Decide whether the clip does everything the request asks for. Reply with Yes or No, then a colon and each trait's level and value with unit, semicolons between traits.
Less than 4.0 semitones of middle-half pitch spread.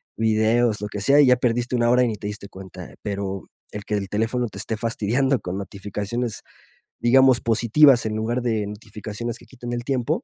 Yes: average, 2.9 semitones